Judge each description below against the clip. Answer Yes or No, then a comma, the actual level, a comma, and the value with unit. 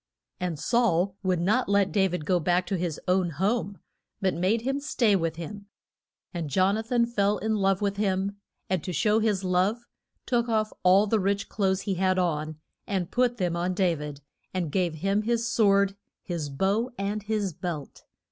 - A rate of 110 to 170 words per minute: No, average, 190 wpm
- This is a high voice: Yes, high, 195 Hz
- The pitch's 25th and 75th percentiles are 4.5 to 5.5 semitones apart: No, average, 3.0 semitones